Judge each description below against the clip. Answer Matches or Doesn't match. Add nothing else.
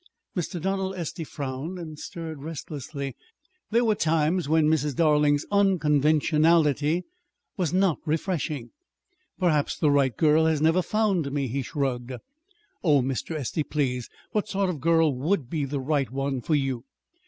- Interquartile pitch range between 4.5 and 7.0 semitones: Doesn't match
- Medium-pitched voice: Matches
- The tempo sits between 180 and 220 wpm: Doesn't match